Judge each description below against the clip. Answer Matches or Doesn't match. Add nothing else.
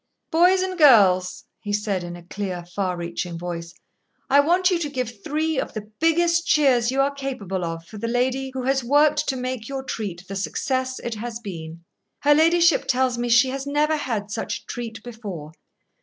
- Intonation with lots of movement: Matches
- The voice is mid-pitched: Doesn't match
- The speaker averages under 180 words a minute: Doesn't match